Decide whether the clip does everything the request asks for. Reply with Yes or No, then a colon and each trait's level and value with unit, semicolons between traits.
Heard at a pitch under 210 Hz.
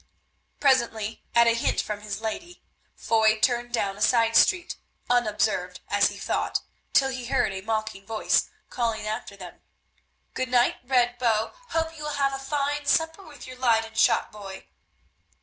No: high, 235 Hz